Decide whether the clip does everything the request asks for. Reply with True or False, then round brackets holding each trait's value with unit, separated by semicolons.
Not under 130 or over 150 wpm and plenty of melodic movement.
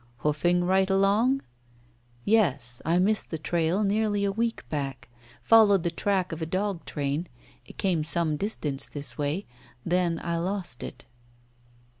False (145 wpm; 4.6 semitones)